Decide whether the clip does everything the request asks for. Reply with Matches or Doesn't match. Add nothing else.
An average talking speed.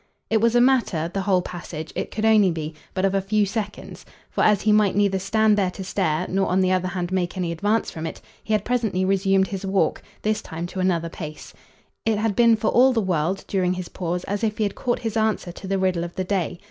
Doesn't match